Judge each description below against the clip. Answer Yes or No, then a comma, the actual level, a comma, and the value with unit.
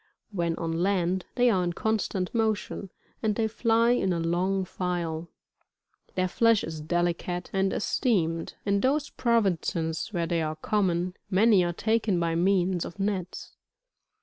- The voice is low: No, medium, 185 Hz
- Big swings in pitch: No, average, 3.8 semitones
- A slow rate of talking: No, average, 150 wpm